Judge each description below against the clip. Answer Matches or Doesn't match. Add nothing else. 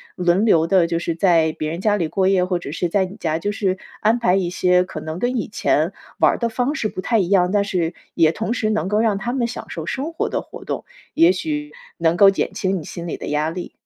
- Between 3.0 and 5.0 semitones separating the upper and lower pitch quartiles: Matches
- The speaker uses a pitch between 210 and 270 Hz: Doesn't match